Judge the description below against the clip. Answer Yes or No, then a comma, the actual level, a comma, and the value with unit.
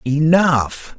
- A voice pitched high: No, medium, 150 Hz